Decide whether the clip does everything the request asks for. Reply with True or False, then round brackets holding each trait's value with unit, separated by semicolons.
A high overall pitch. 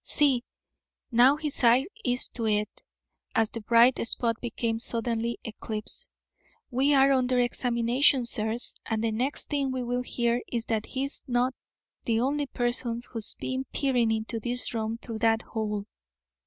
True (240 Hz)